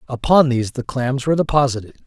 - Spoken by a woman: No, male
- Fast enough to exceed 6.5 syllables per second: Yes, 6.7 syllables/s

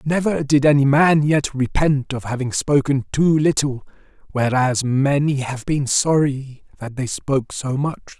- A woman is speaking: No, male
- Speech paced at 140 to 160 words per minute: Yes, average, 155 wpm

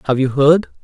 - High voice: No, medium, 145 Hz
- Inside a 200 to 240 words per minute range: Yes, fast, 215 wpm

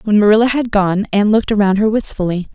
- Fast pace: Yes, fast, 210 wpm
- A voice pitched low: No, high, 210 Hz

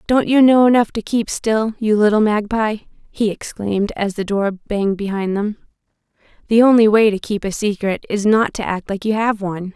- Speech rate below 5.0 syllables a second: No, 5.1 syllables/s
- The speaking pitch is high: Yes, high, 210 Hz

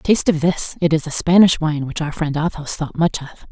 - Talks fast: Yes, fast, 255 wpm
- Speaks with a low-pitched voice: No, medium, 160 Hz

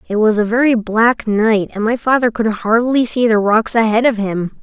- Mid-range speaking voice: No, high, 225 Hz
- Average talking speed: No, fast, 220 wpm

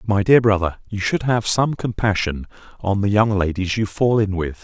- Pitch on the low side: Yes, low, 100 Hz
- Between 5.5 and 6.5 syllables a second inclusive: No, 4.9 syllables/s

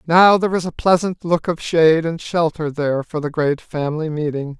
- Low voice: No, medium, 160 Hz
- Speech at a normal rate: No, fast, 210 wpm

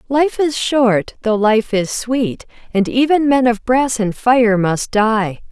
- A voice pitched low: No, high, 235 Hz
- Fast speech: No, average, 175 wpm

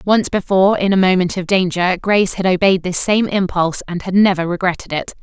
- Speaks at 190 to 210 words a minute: Yes, fast, 205 wpm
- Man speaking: No, female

